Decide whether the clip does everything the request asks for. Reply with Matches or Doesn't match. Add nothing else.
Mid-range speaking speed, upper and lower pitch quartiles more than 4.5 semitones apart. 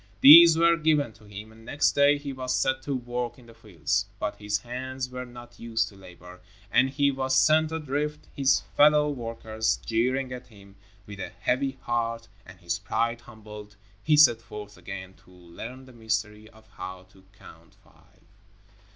Doesn't match